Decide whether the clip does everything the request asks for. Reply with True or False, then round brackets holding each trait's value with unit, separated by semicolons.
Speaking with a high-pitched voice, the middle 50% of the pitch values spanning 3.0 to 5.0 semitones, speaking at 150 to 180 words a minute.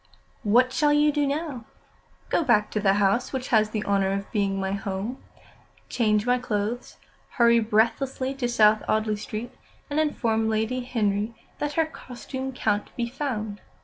True (230 Hz; 3.6 semitones; 160 wpm)